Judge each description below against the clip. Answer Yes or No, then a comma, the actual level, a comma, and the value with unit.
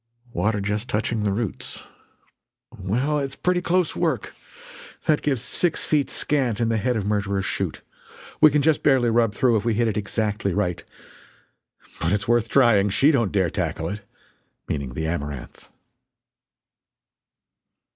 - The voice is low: Yes, low, 110 Hz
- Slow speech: No, average, 150 wpm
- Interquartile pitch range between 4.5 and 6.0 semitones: Yes, average, 5.1 semitones